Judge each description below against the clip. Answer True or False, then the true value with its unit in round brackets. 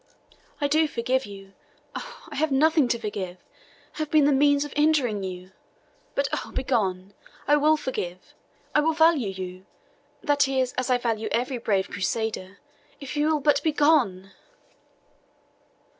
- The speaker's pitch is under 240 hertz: False (260 Hz)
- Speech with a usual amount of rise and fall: False (6.7 semitones)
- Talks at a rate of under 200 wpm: True (150 wpm)